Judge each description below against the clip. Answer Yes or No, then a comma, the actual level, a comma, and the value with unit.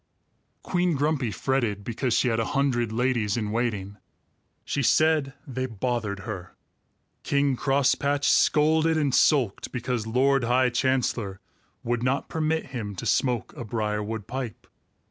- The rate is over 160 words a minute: No, slow, 135 wpm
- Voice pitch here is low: Yes, low, 125 Hz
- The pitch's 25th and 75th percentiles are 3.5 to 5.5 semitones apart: Yes, average, 3.9 semitones